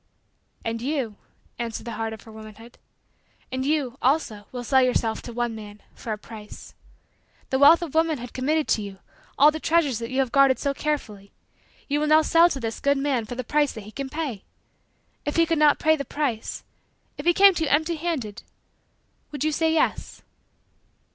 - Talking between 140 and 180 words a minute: No, average, 195 wpm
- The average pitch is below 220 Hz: No, very high, 270 Hz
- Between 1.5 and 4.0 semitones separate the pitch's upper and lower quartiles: No, average, 5.1 semitones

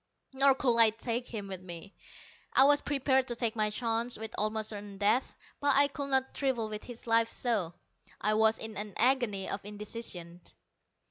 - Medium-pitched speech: No, high, 225 Hz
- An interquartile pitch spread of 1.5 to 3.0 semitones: No, average, 3.5 semitones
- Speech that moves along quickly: No, average, 185 wpm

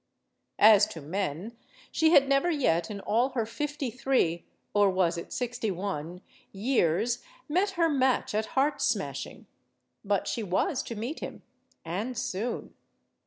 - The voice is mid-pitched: No, high, 220 Hz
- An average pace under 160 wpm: Yes, average, 145 wpm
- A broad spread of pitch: Yes, wide, 6.0 semitones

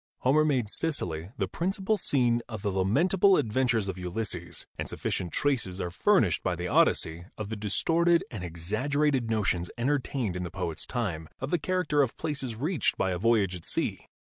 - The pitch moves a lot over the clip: Yes, wide, 8.1 semitones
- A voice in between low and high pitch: No, low, 115 Hz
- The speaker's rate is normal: Yes, average, 175 wpm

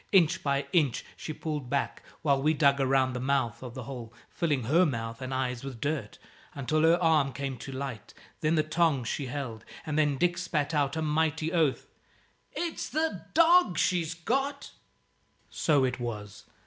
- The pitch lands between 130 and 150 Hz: Yes, medium, 140 Hz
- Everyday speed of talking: Yes, average, 175 wpm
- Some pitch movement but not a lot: Yes, average, 3.7 semitones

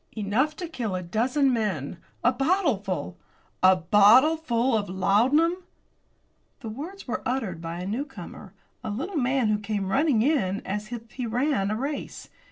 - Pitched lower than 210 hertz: No, high, 230 Hz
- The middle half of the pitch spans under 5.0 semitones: No, wide, 5.5 semitones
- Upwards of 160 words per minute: No, average, 155 wpm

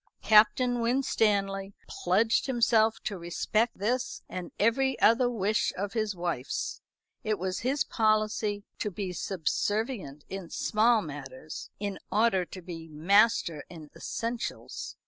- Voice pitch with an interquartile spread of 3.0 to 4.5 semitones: Yes, average, 4.1 semitones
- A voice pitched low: No, high, 205 Hz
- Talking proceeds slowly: Yes, slow, 125 wpm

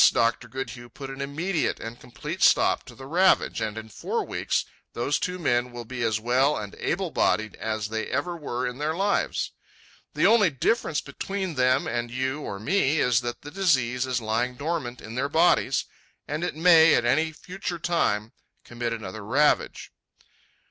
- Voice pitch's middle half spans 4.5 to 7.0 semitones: Yes, average, 5.1 semitones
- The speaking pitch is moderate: No, low, 130 Hz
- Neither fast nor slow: Yes, average, 175 wpm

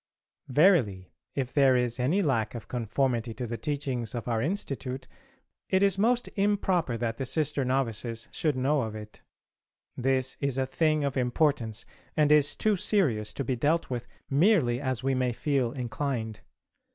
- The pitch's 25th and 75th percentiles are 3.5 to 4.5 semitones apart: Yes, average, 4.0 semitones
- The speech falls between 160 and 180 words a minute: Yes, average, 165 wpm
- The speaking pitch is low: Yes, low, 130 Hz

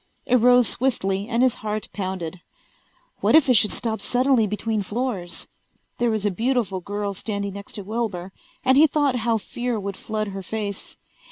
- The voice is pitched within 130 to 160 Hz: No, high, 215 Hz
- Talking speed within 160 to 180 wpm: Yes, average, 175 wpm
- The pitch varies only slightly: No, average, 3.6 semitones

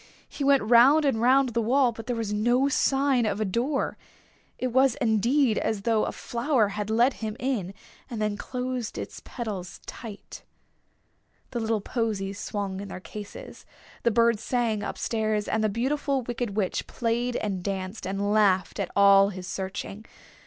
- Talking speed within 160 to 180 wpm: Yes, average, 170 wpm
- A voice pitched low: No, high, 225 Hz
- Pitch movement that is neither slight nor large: Yes, average, 3.4 semitones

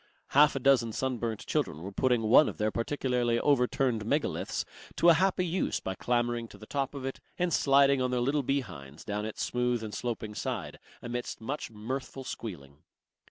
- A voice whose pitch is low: Yes, low, 125 Hz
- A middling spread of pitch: Yes, average, 3.7 semitones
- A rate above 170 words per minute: Yes, average, 180 wpm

